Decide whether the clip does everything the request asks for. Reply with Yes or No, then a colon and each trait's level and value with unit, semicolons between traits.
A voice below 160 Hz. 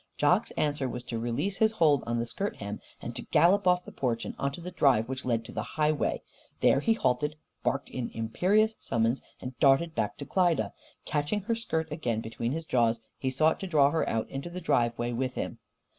Yes: medium, 140 Hz